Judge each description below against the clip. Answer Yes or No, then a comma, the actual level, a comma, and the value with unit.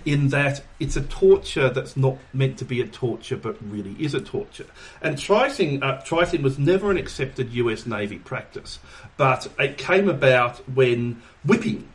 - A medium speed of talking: Yes, average, 165 wpm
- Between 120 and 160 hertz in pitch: Yes, low, 135 Hz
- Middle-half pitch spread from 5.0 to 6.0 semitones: No, average, 4.2 semitones